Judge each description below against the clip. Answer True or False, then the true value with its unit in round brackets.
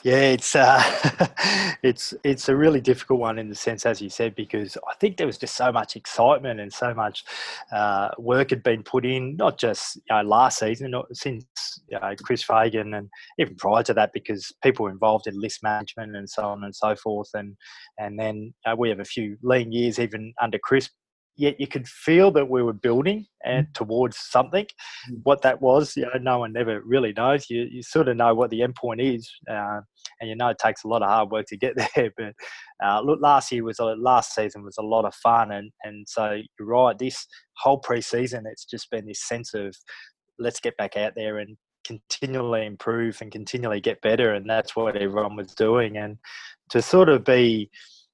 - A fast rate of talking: True (215 wpm)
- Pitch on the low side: True (115 Hz)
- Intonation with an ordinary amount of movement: True (3.0 semitones)